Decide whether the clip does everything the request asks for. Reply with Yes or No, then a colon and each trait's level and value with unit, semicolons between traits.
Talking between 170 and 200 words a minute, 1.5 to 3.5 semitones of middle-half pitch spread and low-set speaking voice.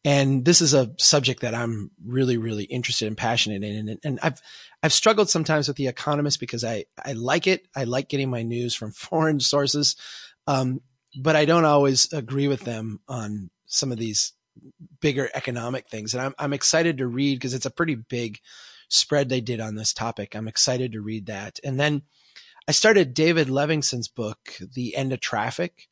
No: average, 190 wpm; average, 4.1 semitones; low, 130 Hz